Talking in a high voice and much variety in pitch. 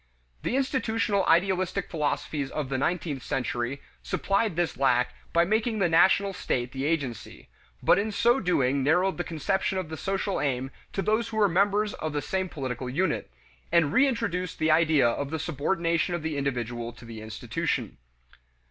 No: medium, 165 Hz; wide, 6.1 semitones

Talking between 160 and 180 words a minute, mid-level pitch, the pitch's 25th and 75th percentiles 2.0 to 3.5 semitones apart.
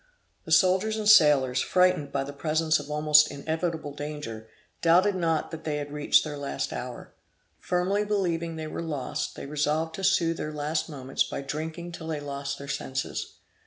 Yes: average, 175 wpm; medium, 155 Hz; average, 2.7 semitones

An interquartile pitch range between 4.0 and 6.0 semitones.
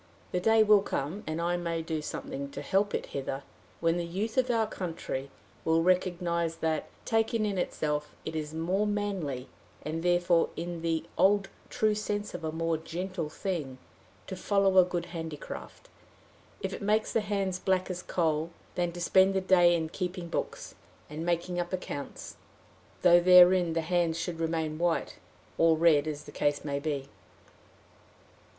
No: average, 2.9 semitones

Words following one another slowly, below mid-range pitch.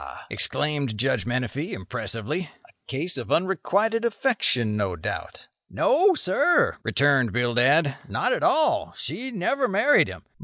No: slow, 125 wpm; medium, 150 Hz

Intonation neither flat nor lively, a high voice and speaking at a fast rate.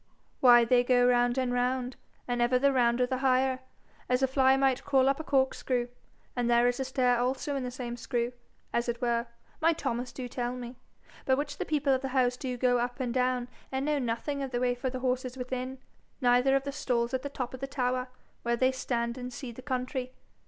No: narrow, 1.4 semitones; very high, 255 Hz; fast, 225 wpm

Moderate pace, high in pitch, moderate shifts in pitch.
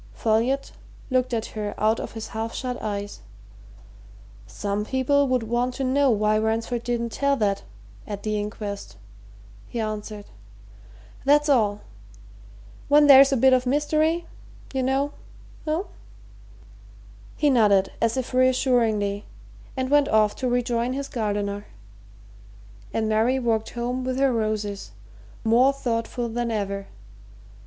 No: slow, 130 wpm; high, 235 Hz; average, 3.5 semitones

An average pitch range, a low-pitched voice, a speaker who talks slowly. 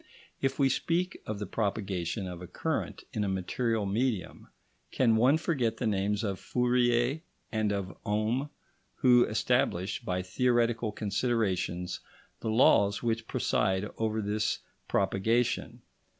Yes: average, 3.6 semitones; low, 110 Hz; slow, 130 wpm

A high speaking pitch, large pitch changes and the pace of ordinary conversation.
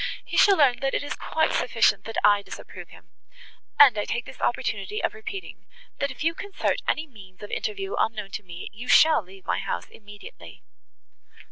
Yes: high, 245 Hz; wide, 8.0 semitones; average, 180 wpm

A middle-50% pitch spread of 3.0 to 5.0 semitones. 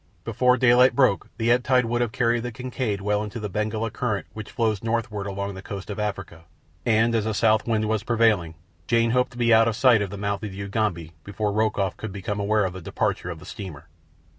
No: narrow, 2.6 semitones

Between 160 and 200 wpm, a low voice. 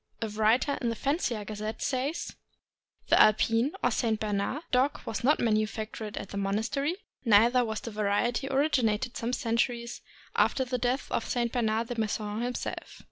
No: average, 165 wpm; high, 230 Hz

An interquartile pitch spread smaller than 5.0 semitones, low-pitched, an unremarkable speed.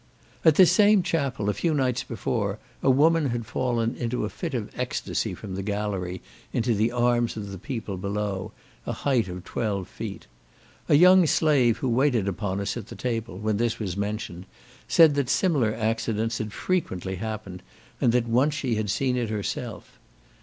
Yes: average, 4.2 semitones; low, 115 Hz; average, 175 wpm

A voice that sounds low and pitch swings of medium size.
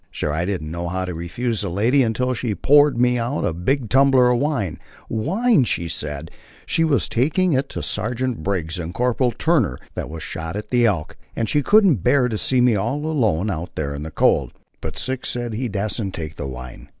No: low, 115 Hz; wide, 7.3 semitones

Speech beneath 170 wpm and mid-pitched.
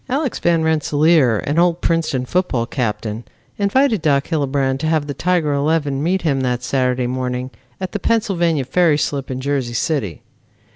Yes: average, 160 wpm; medium, 145 Hz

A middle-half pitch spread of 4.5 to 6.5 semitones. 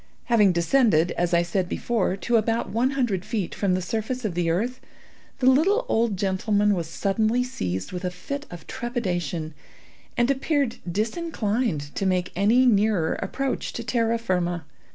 Yes: average, 5.2 semitones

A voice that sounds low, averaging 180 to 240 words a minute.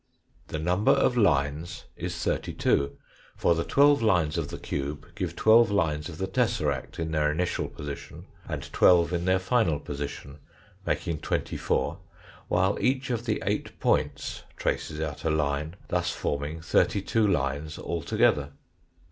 No: very low, 80 Hz; average, 155 wpm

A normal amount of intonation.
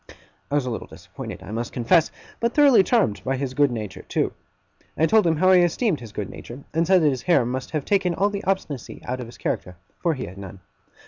No: wide, 7.4 semitones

